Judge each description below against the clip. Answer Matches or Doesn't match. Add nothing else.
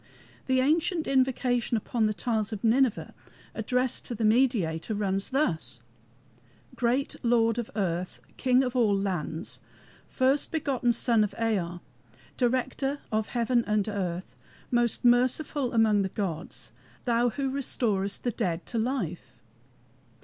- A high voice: Matches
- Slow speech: Matches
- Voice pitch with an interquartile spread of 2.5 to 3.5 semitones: Doesn't match